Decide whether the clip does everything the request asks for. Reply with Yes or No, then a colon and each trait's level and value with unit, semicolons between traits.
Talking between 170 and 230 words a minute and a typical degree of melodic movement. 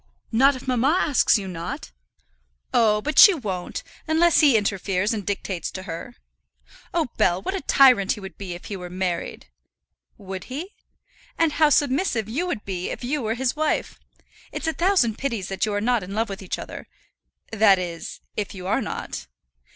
No: average, 185 wpm; wide, 6.4 semitones